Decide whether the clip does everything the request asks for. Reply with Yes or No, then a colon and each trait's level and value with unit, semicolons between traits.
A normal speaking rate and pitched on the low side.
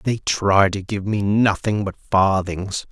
Yes: average, 165 wpm; low, 100 Hz